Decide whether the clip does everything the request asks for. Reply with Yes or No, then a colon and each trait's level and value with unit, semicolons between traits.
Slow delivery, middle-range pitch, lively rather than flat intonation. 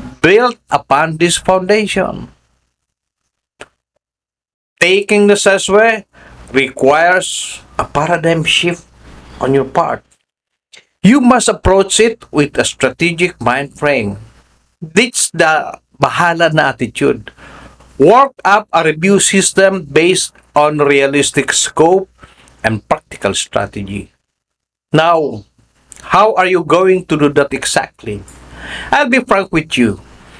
Yes: slow, 105 wpm; medium, 165 Hz; wide, 6.4 semitones